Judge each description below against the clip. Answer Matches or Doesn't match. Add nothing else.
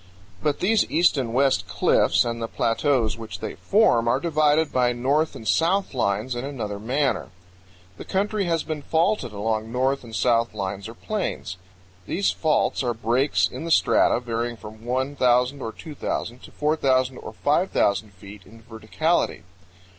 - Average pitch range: Matches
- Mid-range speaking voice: Doesn't match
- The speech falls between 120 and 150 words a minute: Doesn't match